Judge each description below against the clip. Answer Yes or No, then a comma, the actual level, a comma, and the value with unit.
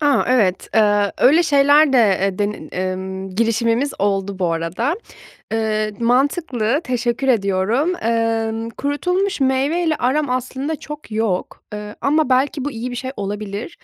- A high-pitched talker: Yes, high, 235 Hz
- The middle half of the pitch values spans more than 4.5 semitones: Yes, average, 5.3 semitones